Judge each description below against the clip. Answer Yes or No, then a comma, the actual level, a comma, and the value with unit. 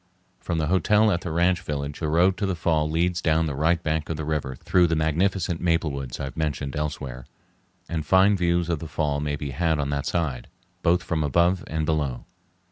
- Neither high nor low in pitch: No, very low, 80 Hz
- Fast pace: Yes, fast, 215 wpm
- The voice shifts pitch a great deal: No, average, 2.8 semitones